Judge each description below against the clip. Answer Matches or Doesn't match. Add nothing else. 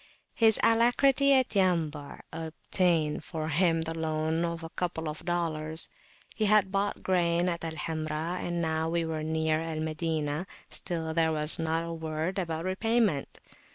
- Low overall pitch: Doesn't match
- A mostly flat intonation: Matches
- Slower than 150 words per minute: Doesn't match